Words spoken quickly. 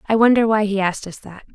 Yes: fast, 270 wpm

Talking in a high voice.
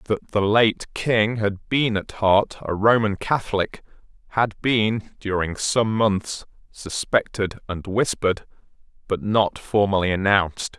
No: low, 105 Hz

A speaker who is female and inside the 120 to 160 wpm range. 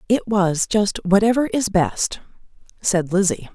Yes: female; slow, 135 wpm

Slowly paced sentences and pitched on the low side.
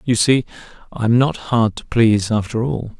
No: average, 200 wpm; low, 115 Hz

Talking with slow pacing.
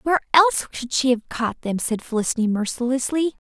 No: average, 170 wpm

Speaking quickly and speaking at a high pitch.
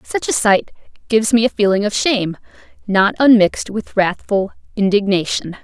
No: average, 150 wpm; high, 210 Hz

